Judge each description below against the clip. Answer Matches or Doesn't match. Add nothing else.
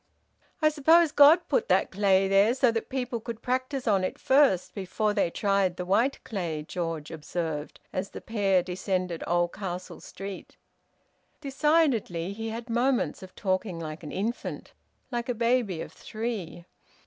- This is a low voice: Doesn't match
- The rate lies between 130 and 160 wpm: Matches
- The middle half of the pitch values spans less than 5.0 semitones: Doesn't match